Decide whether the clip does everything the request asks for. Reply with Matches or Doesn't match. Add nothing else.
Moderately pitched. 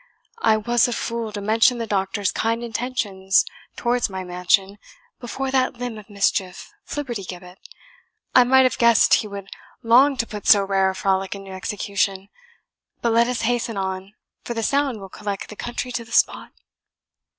Doesn't match